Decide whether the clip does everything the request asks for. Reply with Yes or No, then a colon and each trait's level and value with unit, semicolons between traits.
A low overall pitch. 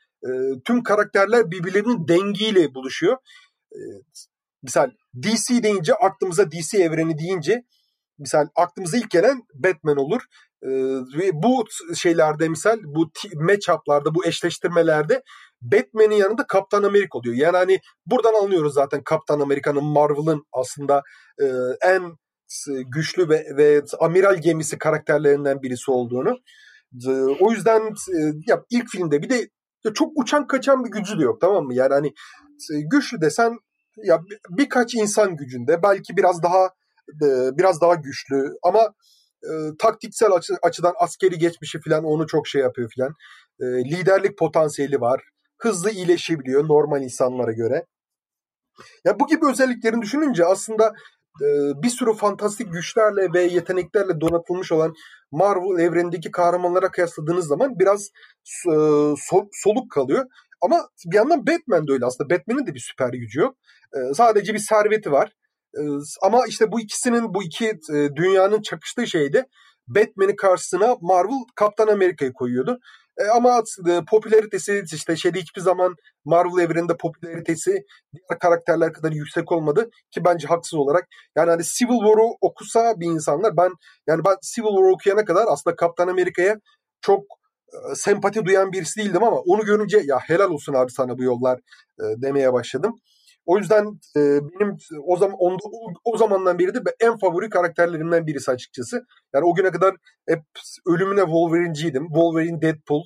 No: medium, 185 Hz